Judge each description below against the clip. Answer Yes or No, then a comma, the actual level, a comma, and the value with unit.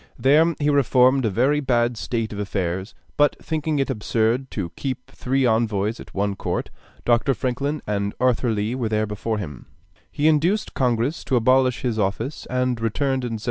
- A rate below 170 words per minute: No, average, 180 wpm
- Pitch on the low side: Yes, low, 125 Hz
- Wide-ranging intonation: No, average, 3.9 semitones